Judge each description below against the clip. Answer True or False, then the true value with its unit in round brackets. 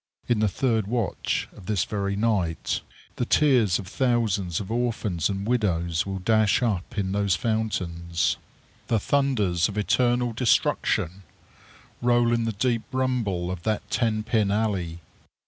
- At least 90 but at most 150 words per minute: True (145 wpm)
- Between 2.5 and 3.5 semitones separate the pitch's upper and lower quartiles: False (4.0 semitones)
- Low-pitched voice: True (105 Hz)